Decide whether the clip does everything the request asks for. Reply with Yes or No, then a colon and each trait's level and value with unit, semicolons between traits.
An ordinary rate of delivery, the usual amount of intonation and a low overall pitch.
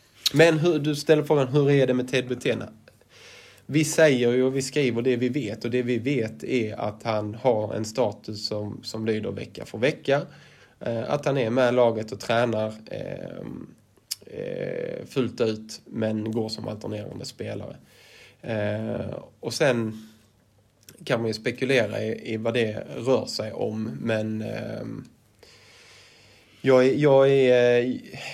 Yes: average, 140 wpm; average, 3.7 semitones; low, 120 Hz